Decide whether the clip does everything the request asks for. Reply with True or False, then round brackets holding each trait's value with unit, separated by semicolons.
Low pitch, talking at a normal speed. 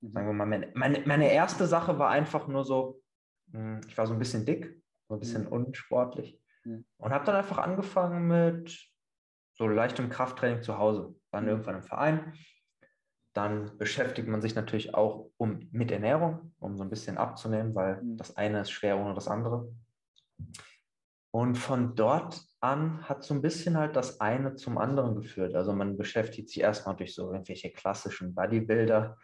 True (115 Hz; 170 wpm)